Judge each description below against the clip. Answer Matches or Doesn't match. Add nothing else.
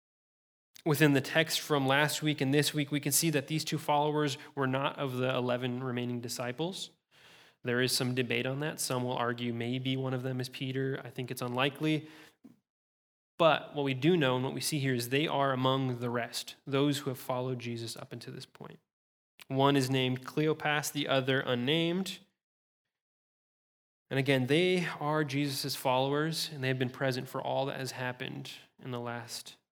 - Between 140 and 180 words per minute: Doesn't match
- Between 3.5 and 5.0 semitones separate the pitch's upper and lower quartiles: Doesn't match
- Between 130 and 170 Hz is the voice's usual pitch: Matches